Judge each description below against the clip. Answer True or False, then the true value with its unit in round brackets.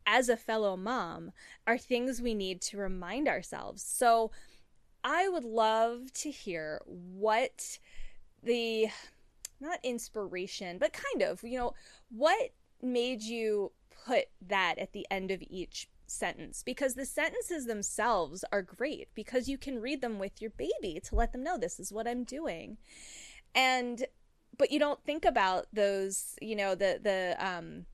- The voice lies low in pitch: False (235 Hz)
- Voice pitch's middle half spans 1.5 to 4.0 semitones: False (4.5 semitones)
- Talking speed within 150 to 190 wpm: True (155 wpm)